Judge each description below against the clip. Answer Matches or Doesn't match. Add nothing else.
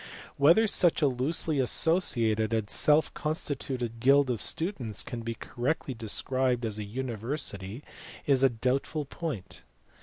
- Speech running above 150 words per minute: Doesn't match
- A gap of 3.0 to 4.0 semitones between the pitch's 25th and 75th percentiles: Doesn't match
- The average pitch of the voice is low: Matches